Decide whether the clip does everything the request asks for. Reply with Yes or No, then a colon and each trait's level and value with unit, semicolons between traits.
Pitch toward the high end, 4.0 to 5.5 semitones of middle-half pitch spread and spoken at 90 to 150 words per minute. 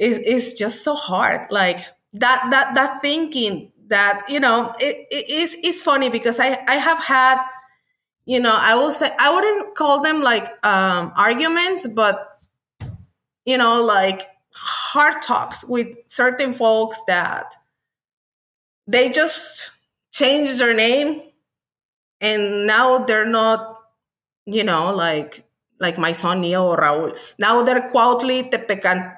Yes: high, 235 Hz; average, 4.7 semitones; slow, 135 wpm